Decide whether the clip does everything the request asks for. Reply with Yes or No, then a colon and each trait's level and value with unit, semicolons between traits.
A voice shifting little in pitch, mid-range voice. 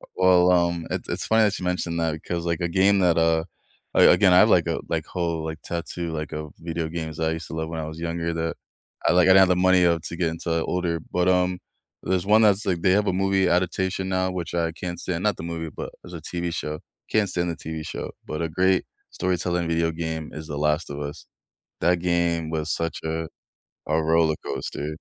No: narrow, 2.0 semitones; very low, 85 Hz